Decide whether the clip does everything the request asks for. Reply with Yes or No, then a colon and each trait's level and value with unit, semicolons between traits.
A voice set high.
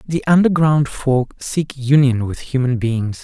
No: low, 135 Hz